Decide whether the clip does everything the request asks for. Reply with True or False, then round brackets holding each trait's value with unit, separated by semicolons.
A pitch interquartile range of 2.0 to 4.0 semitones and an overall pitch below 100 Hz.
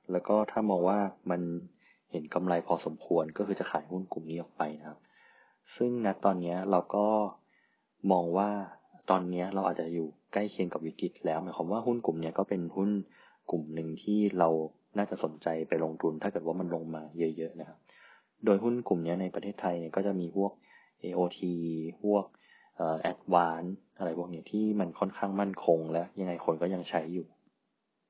True (3.0 semitones; 90 Hz)